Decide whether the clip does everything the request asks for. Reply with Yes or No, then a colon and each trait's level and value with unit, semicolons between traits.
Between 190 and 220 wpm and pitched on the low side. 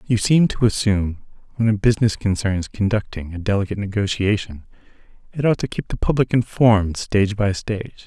No: average, 170 wpm; low, 105 Hz